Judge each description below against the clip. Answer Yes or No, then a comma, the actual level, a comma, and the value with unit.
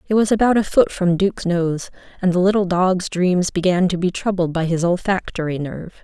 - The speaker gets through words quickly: Yes, fast, 210 wpm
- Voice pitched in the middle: Yes, medium, 180 Hz